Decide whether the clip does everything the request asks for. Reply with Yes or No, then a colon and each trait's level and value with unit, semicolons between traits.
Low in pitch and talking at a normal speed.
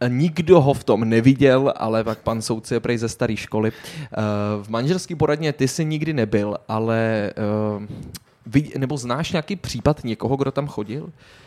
Yes: low, 120 Hz; average, 155 wpm